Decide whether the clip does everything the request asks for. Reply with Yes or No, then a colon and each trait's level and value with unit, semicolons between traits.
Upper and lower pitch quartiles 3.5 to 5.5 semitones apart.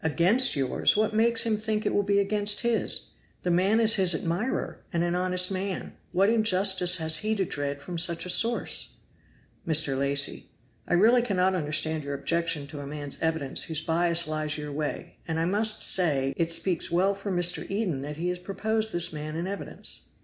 Yes: average, 4.1 semitones